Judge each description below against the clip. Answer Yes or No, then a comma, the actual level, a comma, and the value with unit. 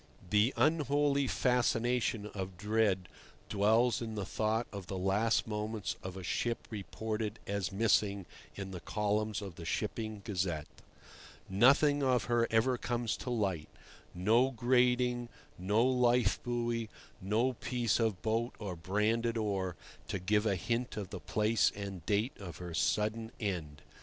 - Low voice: Yes, low, 110 Hz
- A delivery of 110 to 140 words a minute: Yes, slow, 135 wpm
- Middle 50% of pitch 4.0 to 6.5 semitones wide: No, average, 3.3 semitones